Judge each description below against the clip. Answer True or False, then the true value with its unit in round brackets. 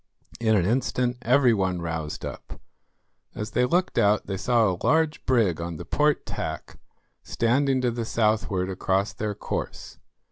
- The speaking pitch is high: False (110 Hz)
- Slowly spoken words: False (155 wpm)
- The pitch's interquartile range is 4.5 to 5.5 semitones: True (4.8 semitones)